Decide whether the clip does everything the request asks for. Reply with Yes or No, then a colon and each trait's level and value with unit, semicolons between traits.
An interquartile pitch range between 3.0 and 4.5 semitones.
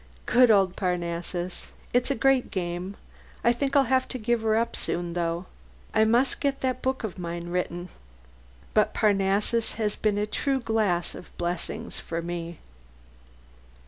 No: wide, 5.4 semitones